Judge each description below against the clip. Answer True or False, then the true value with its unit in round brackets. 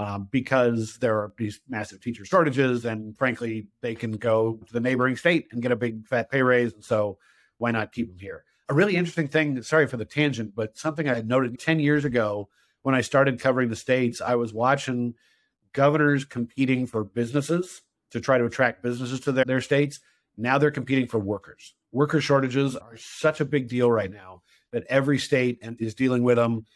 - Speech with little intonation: False (3.3 semitones)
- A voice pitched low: True (125 Hz)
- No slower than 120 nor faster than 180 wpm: False (200 wpm)